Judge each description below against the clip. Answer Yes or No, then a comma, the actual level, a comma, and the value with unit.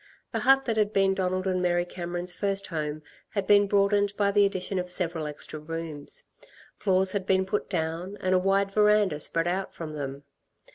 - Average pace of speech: Yes, average, 190 wpm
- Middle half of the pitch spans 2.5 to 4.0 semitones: Yes, average, 3.1 semitones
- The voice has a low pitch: No, medium, 185 Hz